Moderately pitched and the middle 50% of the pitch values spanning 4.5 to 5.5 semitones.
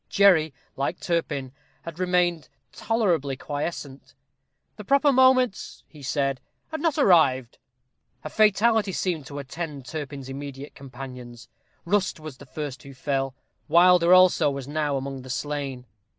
Yes: medium, 150 Hz; average, 5.1 semitones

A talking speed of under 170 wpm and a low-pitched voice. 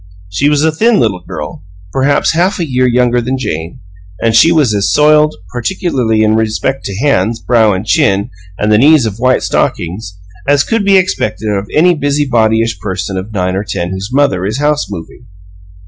No: average, 180 wpm; low, 115 Hz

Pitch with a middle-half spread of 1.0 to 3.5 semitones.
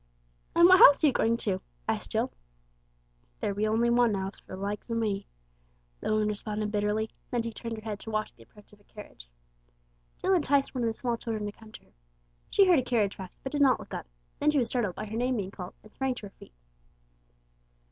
Yes: average, 3.1 semitones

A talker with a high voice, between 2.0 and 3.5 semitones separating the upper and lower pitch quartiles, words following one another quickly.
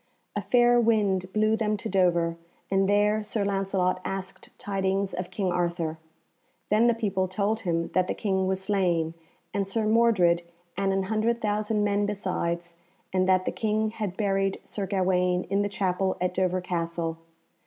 No: high, 195 Hz; narrow, 2.5 semitones; average, 165 wpm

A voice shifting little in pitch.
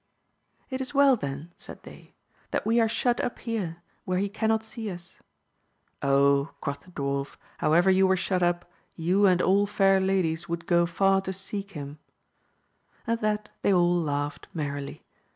No: average, 4.0 semitones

